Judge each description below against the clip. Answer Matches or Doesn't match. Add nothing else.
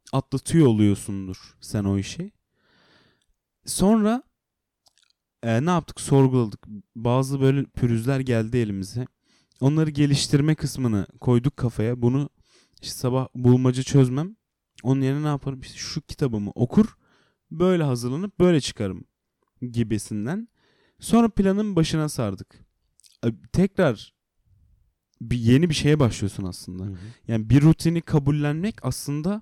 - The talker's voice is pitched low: Matches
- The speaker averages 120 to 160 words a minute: Doesn't match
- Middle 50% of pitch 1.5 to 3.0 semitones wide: Doesn't match